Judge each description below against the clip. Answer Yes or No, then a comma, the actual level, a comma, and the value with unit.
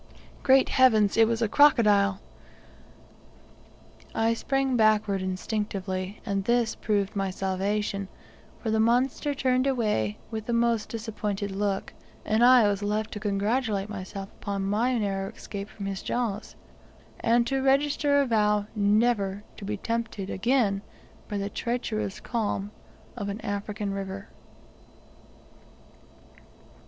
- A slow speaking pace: Yes, slow, 125 wpm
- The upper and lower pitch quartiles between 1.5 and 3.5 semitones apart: Yes, average, 3.0 semitones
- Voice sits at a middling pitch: No, high, 210 Hz